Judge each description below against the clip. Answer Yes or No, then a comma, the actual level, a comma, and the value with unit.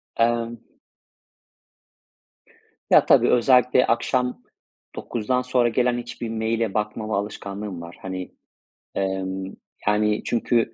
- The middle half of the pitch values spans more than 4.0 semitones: No, average, 3.1 semitones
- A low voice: Yes, low, 115 Hz